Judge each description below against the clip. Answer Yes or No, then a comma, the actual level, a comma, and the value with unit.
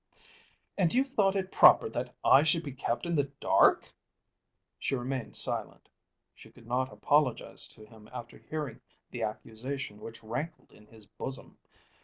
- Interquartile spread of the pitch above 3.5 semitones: Yes, average, 5.2 semitones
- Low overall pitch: Yes, low, 130 Hz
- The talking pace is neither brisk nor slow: Yes, average, 155 wpm